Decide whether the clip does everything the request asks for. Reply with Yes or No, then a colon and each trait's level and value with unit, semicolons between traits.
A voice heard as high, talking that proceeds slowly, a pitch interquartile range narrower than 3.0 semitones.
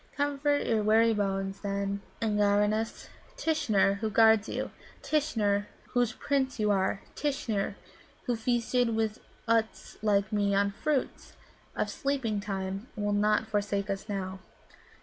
Yes: high, 215 Hz; slow, 130 wpm; narrow, 2.5 semitones